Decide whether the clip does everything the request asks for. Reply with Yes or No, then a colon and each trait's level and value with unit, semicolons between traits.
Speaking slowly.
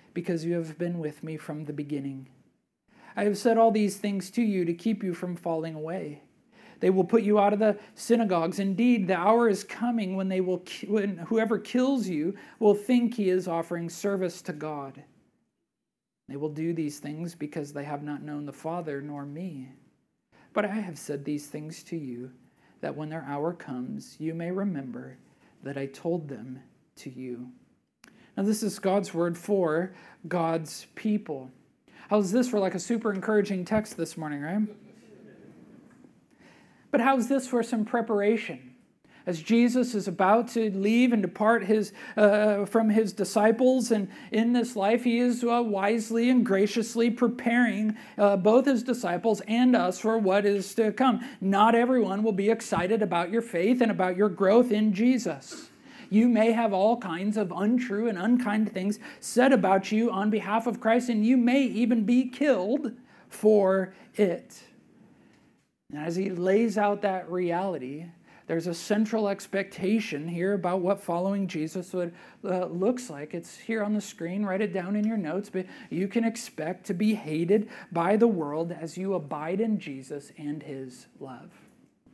No: average, 170 wpm